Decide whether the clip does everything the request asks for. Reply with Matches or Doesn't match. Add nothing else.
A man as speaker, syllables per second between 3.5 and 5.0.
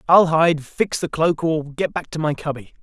Matches